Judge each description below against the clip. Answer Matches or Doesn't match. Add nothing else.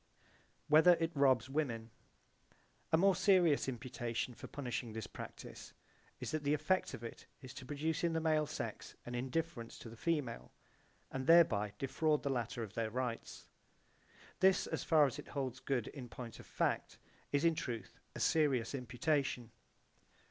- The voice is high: Doesn't match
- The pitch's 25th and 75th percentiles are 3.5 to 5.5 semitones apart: Matches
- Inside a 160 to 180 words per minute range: Matches